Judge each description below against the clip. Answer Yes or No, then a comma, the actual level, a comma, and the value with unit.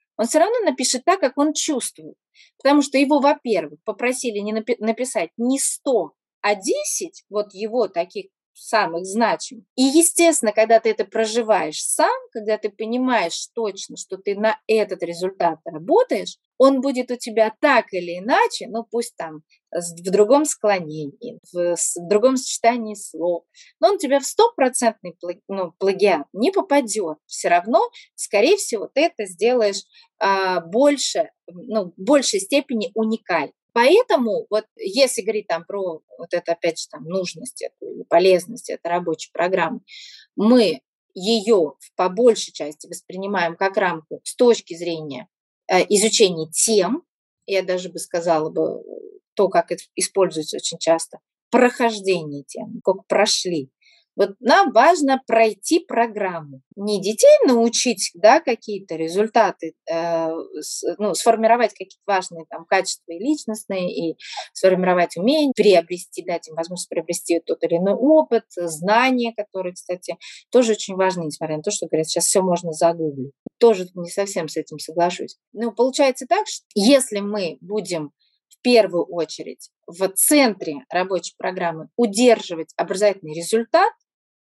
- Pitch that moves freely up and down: Yes, wide, 6.5 semitones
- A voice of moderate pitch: No, high, 210 Hz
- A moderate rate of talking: Yes, average, 140 wpm